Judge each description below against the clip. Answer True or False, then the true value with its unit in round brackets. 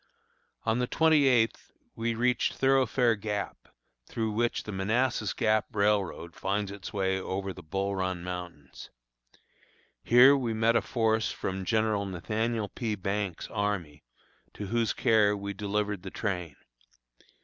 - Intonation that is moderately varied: True (3.1 semitones)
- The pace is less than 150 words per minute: True (140 wpm)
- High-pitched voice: False (105 Hz)